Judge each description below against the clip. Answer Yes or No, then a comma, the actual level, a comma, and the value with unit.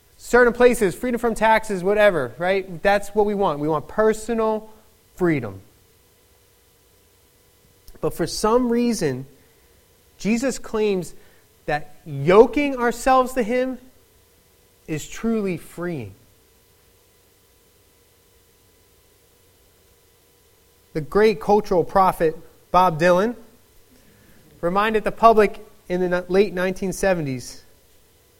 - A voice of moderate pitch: Yes, medium, 180 Hz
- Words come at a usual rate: No, slow, 90 wpm